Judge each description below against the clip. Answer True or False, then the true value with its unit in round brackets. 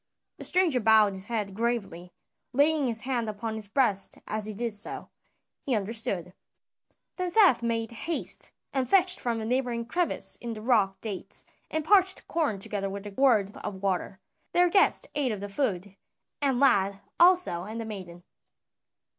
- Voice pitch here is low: False (225 Hz)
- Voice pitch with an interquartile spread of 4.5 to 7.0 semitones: True (5.2 semitones)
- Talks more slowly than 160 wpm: False (165 wpm)